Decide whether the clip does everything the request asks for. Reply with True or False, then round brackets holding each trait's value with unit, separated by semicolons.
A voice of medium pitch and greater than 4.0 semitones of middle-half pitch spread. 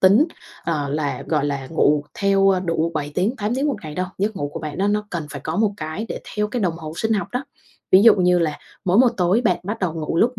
True (180 Hz; 5.1 semitones)